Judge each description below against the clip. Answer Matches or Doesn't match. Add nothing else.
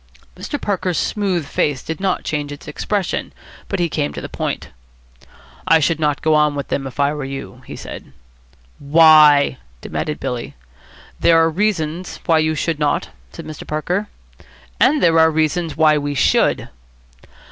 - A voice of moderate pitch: Matches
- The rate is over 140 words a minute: Matches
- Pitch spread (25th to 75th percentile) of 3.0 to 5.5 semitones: Doesn't match